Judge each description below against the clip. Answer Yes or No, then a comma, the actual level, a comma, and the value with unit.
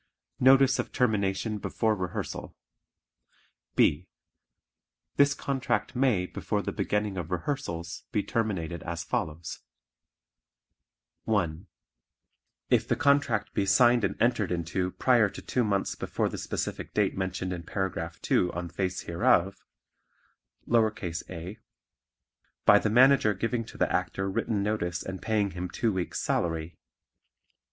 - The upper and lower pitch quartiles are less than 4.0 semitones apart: No, average, 4.5 semitones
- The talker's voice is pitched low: Yes, low, 100 Hz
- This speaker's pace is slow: Yes, slow, 125 wpm